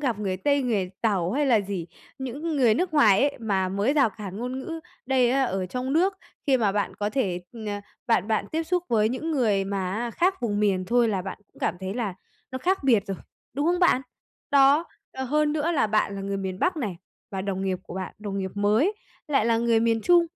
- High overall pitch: Yes, high, 230 Hz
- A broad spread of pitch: Yes, wide, 5.9 semitones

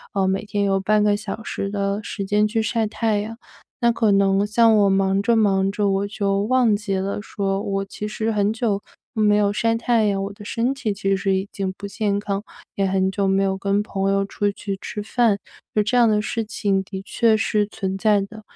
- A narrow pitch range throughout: Yes, narrow, 1.7 semitones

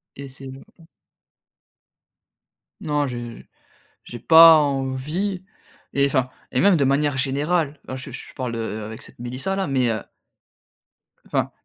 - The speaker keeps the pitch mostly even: No, average, 3.0 semitones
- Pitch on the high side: No, low, 135 Hz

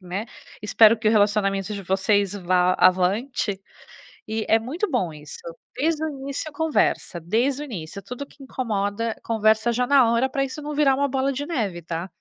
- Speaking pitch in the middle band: No, high, 225 Hz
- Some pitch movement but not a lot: No, wide, 5.7 semitones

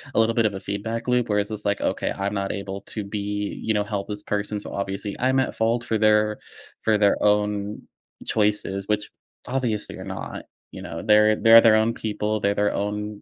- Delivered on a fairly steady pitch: Yes, narrow, 1.4 semitones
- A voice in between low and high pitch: No, low, 105 Hz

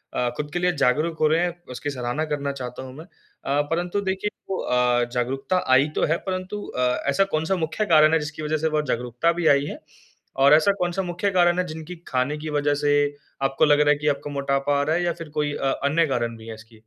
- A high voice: No, medium, 150 Hz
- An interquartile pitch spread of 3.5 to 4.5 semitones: Yes, average, 3.8 semitones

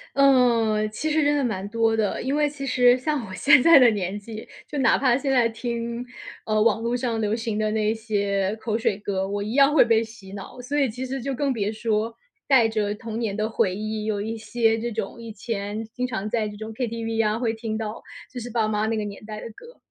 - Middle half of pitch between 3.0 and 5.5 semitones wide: No, narrow, 2.5 semitones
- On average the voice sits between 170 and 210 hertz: No, high, 225 Hz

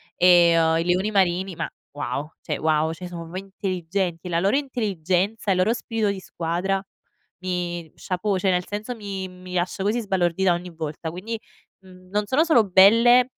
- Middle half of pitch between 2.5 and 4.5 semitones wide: Yes, average, 2.8 semitones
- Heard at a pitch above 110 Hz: Yes, medium, 185 Hz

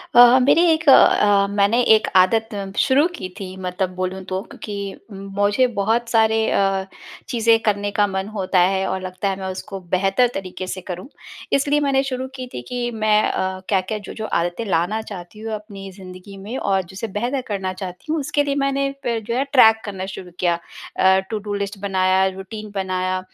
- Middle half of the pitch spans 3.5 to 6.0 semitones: No, average, 3.1 semitones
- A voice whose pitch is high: Yes, high, 200 Hz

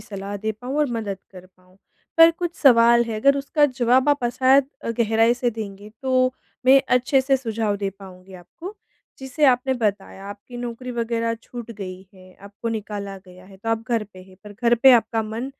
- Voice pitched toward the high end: Yes, high, 230 Hz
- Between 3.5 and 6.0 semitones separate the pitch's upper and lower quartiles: Yes, average, 4.1 semitones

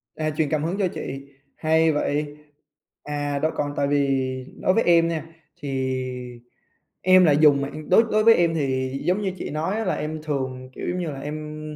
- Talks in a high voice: No, medium, 150 Hz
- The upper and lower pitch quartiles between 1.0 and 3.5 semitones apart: Yes, average, 3.1 semitones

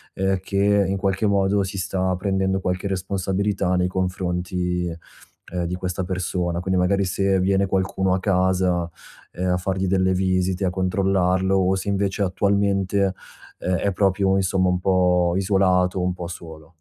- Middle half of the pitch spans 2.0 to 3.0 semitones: No, narrow, 1.2 semitones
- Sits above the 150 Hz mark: No, very low, 95 Hz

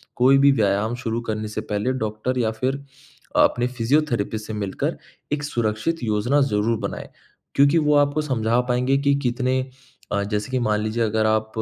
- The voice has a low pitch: Yes, low, 120 Hz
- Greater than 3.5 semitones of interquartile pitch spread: Yes, average, 3.9 semitones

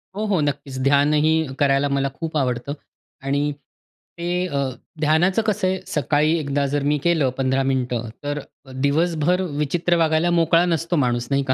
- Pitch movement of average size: Yes, average, 3.4 semitones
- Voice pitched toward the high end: No, medium, 150 Hz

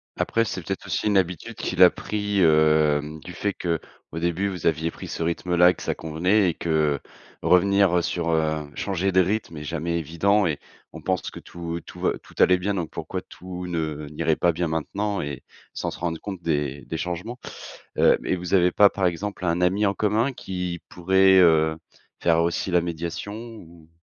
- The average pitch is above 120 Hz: No, very low, 85 Hz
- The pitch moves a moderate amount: Yes, average, 3.0 semitones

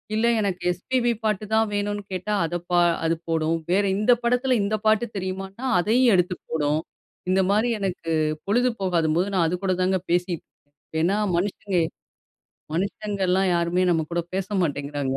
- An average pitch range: Yes, average, 3.2 semitones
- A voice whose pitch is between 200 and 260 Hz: No, high, 190 Hz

